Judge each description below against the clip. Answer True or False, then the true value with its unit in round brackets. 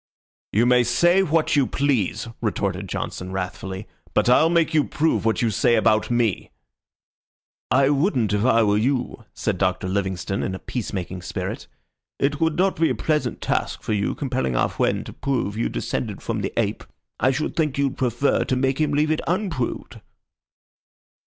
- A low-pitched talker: True (125 Hz)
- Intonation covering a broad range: True (6.0 semitones)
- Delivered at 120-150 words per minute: False (180 wpm)